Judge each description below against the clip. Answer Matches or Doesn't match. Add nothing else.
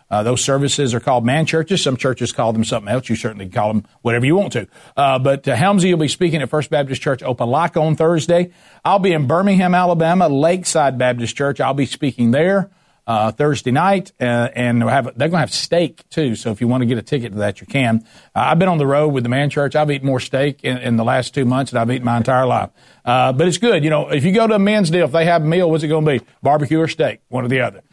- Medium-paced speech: Doesn't match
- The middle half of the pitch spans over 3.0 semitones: Matches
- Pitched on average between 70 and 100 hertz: Doesn't match